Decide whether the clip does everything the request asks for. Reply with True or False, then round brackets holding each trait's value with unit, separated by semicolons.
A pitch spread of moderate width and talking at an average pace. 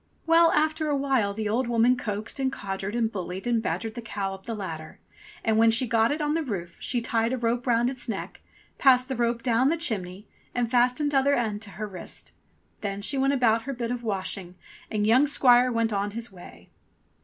False (3.7 semitones; 225 wpm)